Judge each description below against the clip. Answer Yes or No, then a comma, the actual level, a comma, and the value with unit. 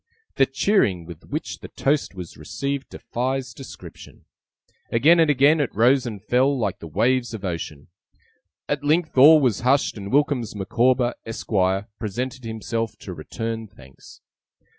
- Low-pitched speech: Yes, low, 120 Hz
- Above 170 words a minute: No, average, 145 wpm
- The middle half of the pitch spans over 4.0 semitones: Yes, average, 4.8 semitones